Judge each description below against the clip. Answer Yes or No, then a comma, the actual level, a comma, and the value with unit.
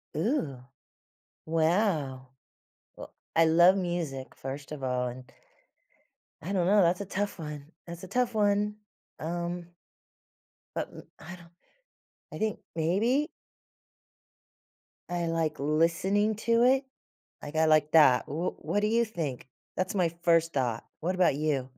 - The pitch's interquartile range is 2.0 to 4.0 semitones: No, average, 4.7 semitones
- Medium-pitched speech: Yes, medium, 170 Hz